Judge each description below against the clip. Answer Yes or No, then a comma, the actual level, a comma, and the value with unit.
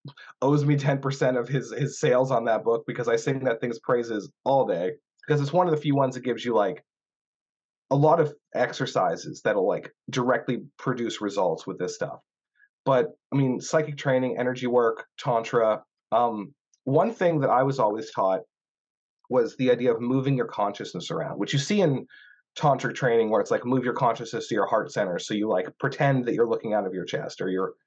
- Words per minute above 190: Yes, fast, 205 wpm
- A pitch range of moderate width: Yes, average, 4.1 semitones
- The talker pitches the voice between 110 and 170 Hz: Yes, low, 135 Hz